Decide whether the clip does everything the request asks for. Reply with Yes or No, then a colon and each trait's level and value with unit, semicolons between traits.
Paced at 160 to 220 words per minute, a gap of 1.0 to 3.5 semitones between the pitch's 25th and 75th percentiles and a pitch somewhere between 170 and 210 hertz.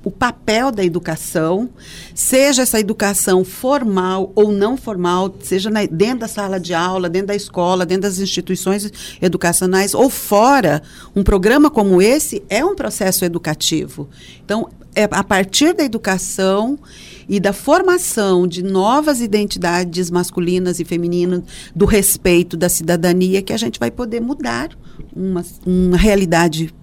No: average, 140 wpm; average, 3.0 semitones; high, 190 Hz